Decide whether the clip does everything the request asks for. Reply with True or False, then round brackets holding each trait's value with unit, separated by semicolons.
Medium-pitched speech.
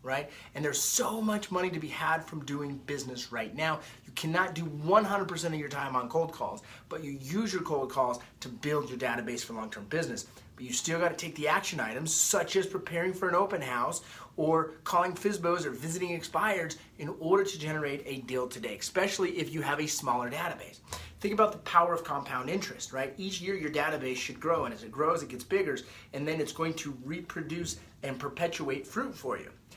True (160 Hz)